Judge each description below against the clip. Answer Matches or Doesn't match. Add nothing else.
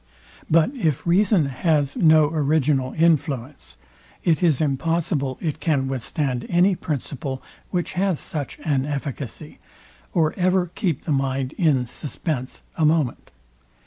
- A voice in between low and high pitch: Matches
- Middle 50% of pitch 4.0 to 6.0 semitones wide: Doesn't match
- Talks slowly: Matches